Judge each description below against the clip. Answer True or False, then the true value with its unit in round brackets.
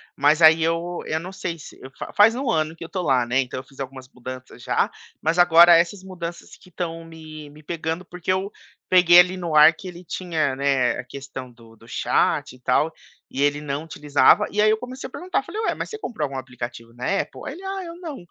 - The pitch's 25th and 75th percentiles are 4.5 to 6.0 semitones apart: True (5.1 semitones)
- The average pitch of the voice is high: False (160 Hz)